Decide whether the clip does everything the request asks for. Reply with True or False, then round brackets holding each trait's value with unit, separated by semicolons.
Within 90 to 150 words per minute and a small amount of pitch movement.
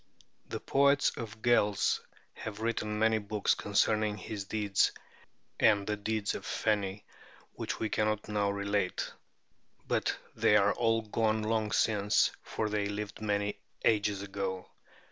True (145 wpm; 1.3 semitones)